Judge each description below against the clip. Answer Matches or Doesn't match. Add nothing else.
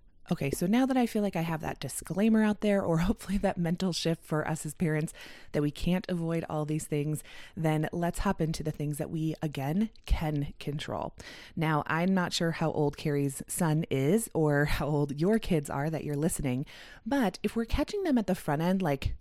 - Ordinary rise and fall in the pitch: Matches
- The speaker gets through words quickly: Matches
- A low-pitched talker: Doesn't match